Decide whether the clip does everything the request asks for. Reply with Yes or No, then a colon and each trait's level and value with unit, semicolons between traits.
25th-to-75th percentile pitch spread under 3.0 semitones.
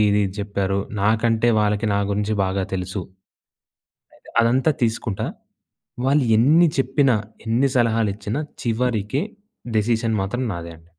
No: average, 3.3 semitones